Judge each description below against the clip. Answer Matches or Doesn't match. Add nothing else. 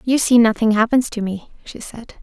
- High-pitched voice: Matches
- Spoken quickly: Matches